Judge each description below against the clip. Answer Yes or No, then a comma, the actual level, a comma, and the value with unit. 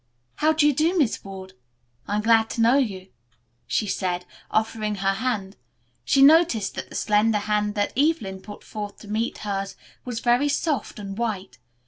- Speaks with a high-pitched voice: Yes, high, 215 Hz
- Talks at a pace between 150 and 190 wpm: Yes, average, 175 wpm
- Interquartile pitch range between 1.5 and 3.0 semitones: No, average, 4.2 semitones